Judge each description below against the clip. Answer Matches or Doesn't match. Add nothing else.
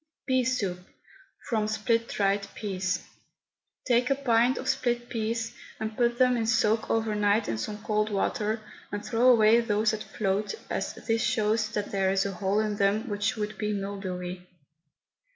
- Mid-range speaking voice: Doesn't match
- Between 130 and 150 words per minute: Doesn't match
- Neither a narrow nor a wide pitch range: Doesn't match